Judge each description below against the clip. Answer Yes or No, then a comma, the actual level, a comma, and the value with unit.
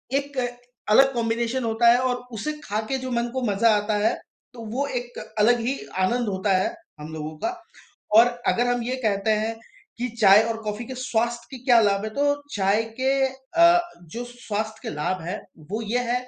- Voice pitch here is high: Yes, high, 235 Hz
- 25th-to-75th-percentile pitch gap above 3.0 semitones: Yes, average, 3.5 semitones